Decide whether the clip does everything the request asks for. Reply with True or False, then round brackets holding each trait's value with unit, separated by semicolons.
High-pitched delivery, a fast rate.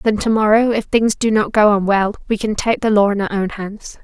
True (210 Hz; 270 wpm)